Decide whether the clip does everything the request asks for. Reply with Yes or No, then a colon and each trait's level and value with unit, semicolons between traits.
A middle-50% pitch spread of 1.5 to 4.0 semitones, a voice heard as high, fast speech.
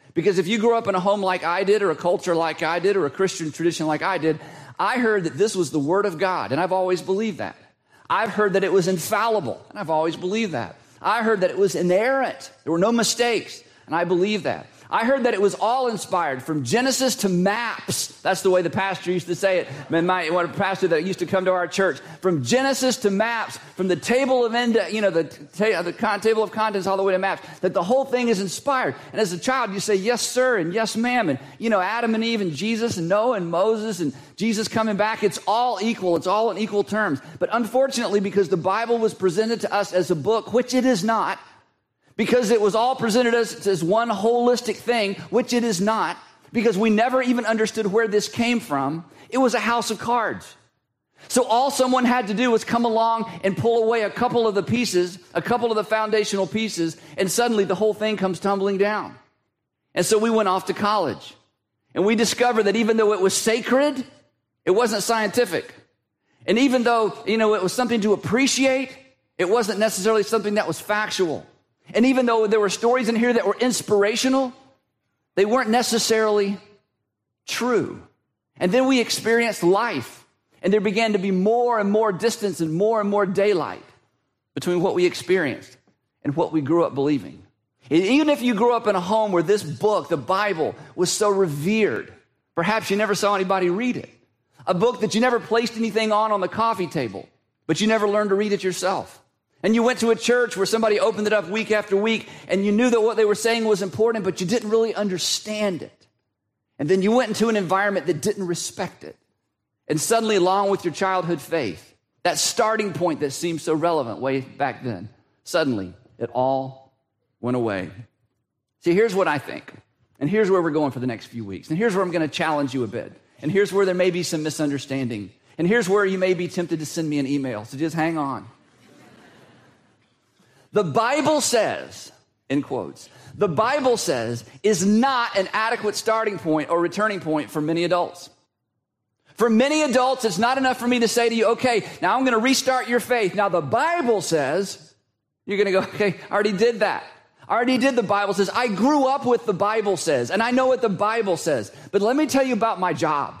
No: average, 4.8 semitones; high, 205 Hz; fast, 215 wpm